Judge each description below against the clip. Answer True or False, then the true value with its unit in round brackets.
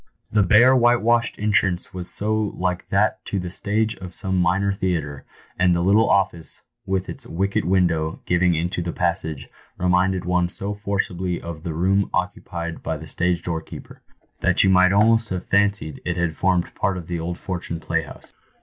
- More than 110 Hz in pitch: False (90 Hz)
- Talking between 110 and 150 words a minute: False (180 wpm)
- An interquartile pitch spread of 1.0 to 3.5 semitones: True (2.5 semitones)